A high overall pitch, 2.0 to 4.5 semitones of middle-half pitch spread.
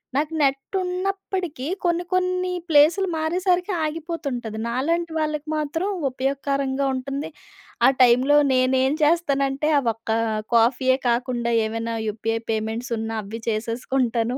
No: very high, 275 Hz; average, 5.3 semitones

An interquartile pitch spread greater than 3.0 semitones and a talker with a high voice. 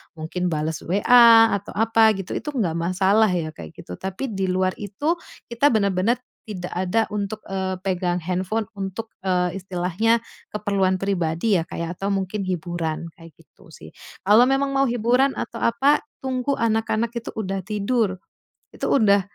Yes: average, 3.9 semitones; high, 195 Hz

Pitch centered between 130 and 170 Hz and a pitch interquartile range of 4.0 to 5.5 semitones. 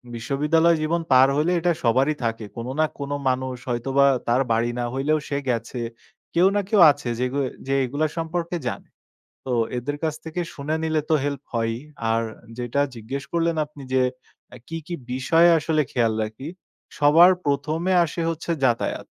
Yes: medium, 140 Hz; average, 4.5 semitones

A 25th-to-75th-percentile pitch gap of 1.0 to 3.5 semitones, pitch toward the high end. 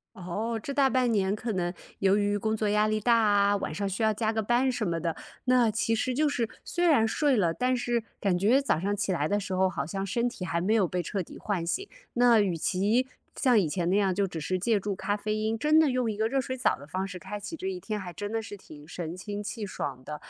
No: average, 4.0 semitones; high, 210 Hz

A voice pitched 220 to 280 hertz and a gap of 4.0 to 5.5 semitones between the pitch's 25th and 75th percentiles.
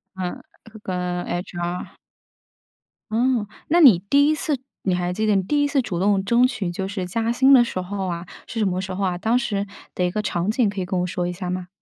No: high, 195 Hz; average, 4.4 semitones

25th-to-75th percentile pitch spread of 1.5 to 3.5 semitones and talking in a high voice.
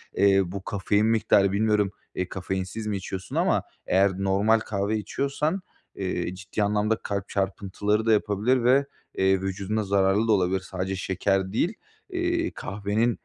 No: narrow, 2.4 semitones; low, 100 Hz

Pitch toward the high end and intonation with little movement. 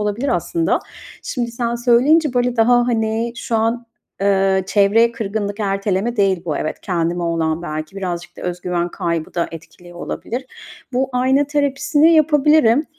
No: high, 225 Hz; wide, 5.6 semitones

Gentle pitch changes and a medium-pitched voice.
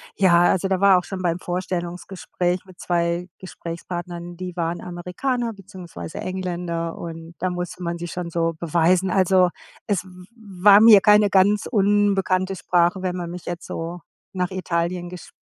Yes: narrow, 1.6 semitones; medium, 180 Hz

